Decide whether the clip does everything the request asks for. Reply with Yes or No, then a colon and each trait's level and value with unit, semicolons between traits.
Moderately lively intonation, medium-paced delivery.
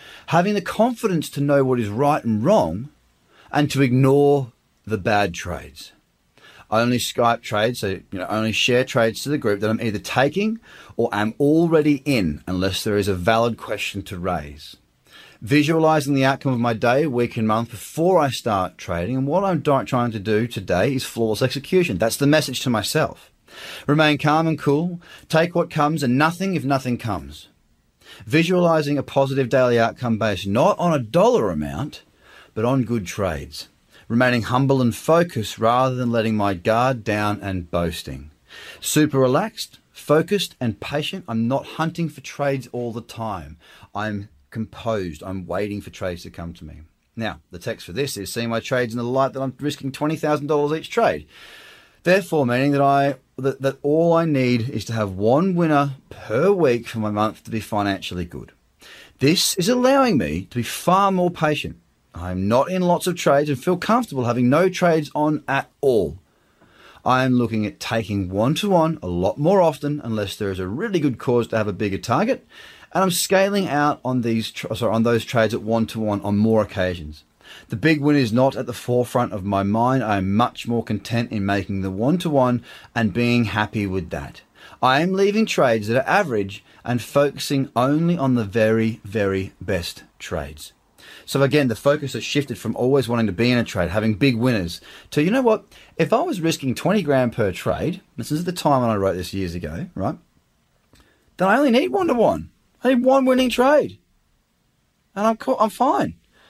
No: wide, 5.8 semitones; average, 190 wpm